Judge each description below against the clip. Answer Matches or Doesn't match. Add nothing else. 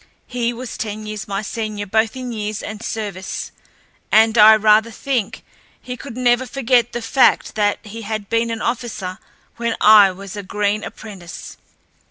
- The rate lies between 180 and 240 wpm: Doesn't match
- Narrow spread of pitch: Matches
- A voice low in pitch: Doesn't match